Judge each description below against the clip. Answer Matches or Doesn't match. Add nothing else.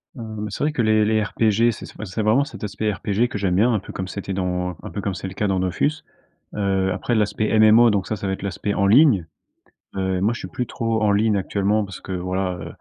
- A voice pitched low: Matches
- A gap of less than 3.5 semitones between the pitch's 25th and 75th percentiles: Matches